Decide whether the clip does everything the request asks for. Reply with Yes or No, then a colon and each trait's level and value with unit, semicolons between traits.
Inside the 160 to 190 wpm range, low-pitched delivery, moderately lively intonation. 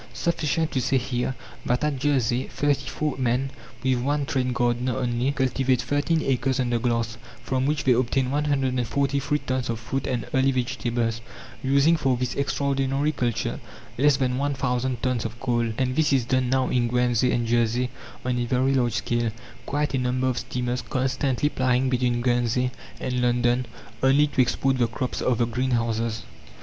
No: average, 170 wpm; low, 130 Hz; narrow, 1.9 semitones